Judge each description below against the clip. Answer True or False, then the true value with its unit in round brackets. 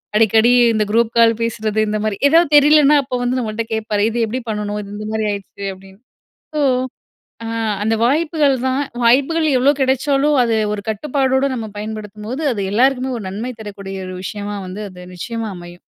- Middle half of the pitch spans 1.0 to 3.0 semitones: False (4.1 semitones)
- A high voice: True (225 Hz)